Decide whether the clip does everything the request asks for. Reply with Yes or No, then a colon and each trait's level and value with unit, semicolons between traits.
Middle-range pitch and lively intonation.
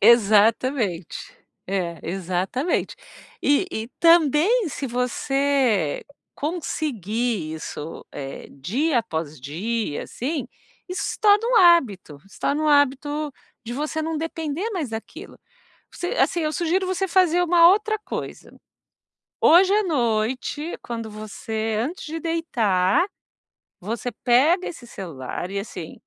No: very high, 260 Hz; wide, 7.9 semitones